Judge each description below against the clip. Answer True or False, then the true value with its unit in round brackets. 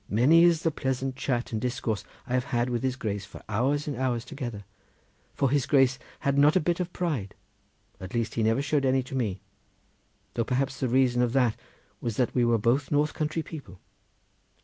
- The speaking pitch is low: True (130 Hz)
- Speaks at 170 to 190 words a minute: False (200 wpm)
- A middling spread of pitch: True (3.3 semitones)